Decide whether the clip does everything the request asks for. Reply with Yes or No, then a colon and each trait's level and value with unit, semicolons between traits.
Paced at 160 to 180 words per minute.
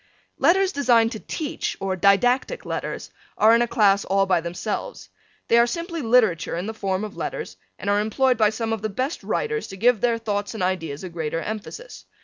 No: average, 200 wpm